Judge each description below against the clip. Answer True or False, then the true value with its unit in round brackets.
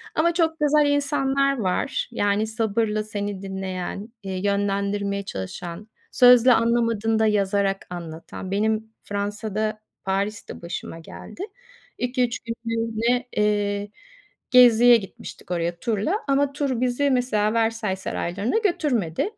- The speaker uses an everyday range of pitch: True (3.7 semitones)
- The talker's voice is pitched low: False (215 Hz)